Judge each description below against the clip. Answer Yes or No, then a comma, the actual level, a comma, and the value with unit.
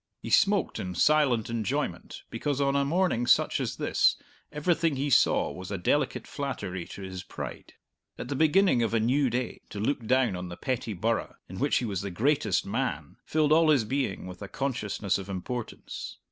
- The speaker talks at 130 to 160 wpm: No, average, 190 wpm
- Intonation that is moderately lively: No, wide, 6.4 semitones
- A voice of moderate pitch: No, low, 125 Hz